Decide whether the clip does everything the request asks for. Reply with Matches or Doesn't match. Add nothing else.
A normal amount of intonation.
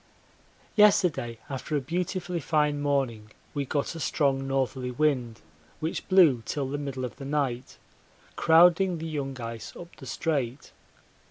Matches